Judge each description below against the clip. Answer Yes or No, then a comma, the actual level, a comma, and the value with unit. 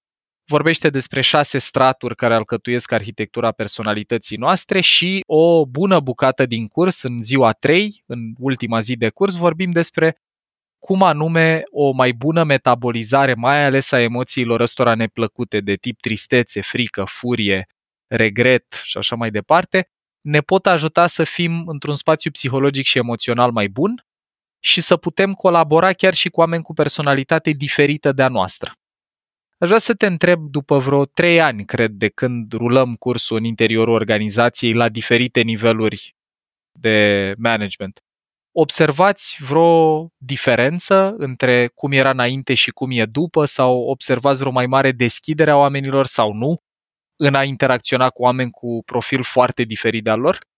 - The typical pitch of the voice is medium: No, low, 130 Hz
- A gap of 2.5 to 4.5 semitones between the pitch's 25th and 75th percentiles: No, average, 5.3 semitones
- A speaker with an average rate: Yes, average, 150 wpm